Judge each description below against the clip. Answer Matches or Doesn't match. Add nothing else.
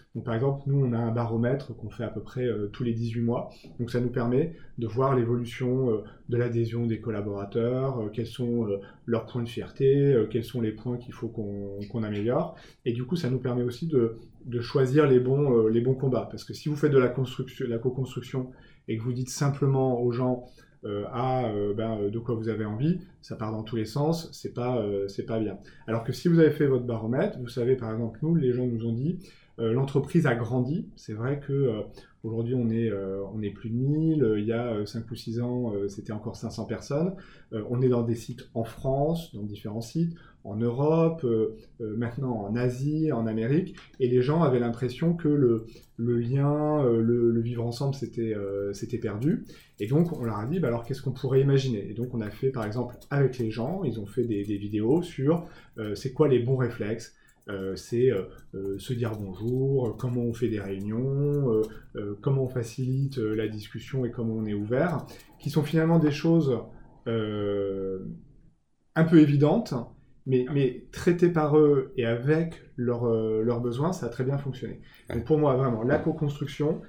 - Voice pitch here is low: Matches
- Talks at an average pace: Matches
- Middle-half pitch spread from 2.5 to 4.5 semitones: Matches